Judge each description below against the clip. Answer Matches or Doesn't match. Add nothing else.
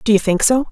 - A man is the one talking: Doesn't match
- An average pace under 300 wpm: Doesn't match